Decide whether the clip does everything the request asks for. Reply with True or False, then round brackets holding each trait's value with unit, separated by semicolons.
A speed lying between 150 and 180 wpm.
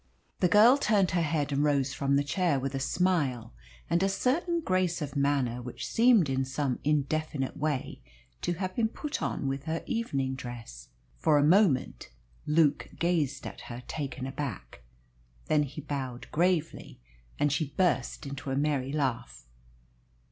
True (160 wpm)